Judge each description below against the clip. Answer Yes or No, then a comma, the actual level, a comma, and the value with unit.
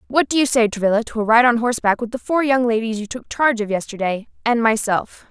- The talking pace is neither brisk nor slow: No, fast, 250 wpm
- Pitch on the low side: No, high, 230 Hz